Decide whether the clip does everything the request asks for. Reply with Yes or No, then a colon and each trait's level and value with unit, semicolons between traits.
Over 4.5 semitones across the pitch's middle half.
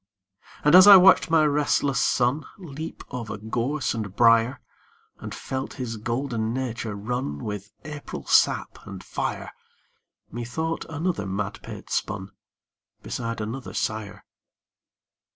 Yes: average, 5.0 semitones